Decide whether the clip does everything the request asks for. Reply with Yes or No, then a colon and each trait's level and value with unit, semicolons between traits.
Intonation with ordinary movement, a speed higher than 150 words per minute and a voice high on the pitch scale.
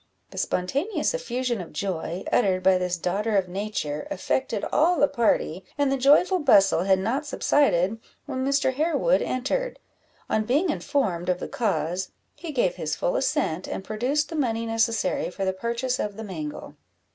No: wide, 7.0 semitones; average, 170 wpm; high, 225 Hz